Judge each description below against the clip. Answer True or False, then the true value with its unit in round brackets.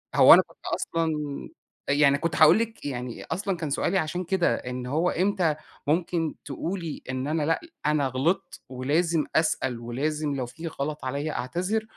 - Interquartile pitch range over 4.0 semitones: False (3.7 semitones)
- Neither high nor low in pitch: True (155 Hz)